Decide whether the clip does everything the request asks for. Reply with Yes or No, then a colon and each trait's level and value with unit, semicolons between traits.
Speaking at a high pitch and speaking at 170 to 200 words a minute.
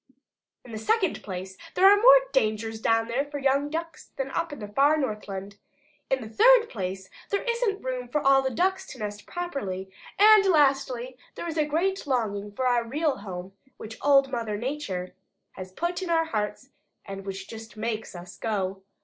Yes: very high, 255 Hz; average, 185 wpm